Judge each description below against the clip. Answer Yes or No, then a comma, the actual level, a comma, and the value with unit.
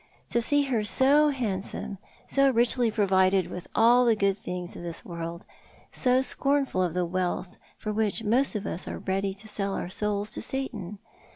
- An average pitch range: Yes, average, 4.7 semitones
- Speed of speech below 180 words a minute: No, average, 185 wpm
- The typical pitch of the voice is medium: No, high, 210 Hz